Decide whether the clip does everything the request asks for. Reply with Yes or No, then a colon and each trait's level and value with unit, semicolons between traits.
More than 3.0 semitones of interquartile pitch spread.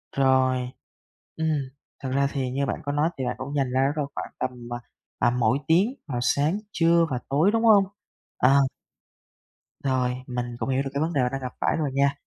No: narrow, 2.6 semitones